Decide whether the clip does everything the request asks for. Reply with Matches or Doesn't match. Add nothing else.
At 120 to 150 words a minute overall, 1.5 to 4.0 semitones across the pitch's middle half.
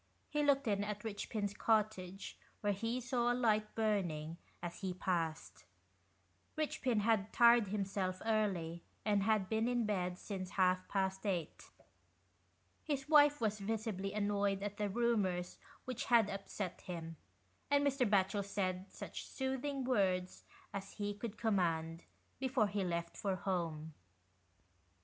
Matches